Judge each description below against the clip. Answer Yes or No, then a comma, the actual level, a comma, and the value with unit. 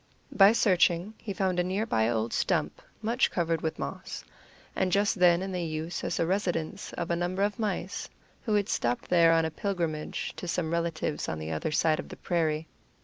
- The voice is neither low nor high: Yes, medium, 175 Hz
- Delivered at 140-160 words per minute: No, average, 195 wpm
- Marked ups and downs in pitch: No, average, 3.2 semitones